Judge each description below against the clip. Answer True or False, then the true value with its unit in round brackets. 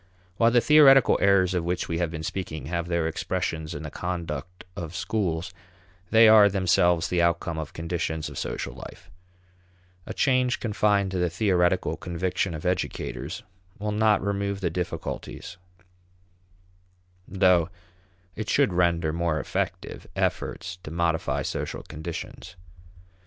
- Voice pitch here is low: True (90 Hz)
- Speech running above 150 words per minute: False (135 wpm)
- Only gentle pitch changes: False (3.2 semitones)